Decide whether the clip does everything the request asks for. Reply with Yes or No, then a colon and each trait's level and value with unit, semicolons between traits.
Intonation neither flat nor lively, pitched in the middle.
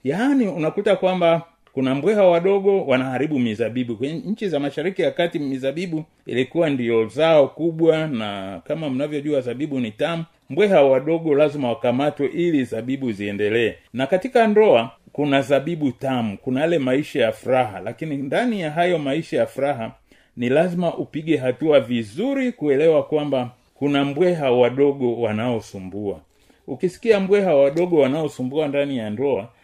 Yes: average, 5.0 semitones; medium, 145 Hz